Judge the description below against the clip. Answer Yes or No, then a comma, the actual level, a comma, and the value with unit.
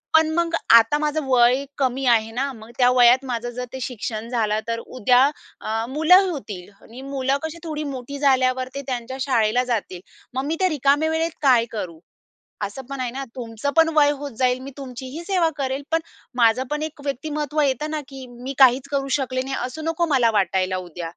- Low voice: No, very high, 260 Hz